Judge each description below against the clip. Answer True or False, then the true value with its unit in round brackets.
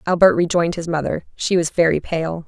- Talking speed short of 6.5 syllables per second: True (5.8 syllables/s)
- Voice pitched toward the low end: False (165 Hz)